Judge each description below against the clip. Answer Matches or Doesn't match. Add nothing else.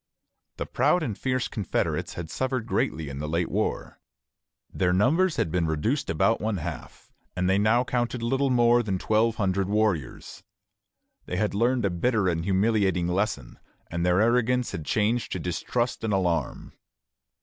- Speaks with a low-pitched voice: Matches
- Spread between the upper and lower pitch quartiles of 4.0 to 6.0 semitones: Matches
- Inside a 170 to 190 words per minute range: Doesn't match